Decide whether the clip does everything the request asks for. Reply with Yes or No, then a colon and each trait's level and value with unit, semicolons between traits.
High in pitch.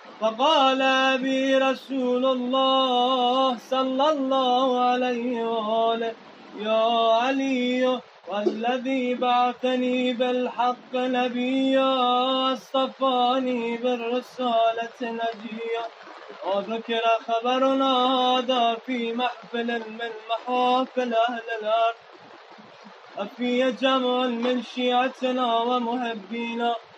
Yes: very high, 250 Hz